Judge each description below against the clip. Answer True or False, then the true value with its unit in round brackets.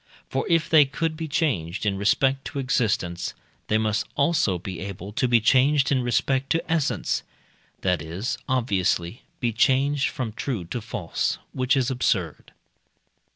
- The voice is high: False (120 Hz)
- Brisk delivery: False (155 wpm)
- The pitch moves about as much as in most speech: False (5.8 semitones)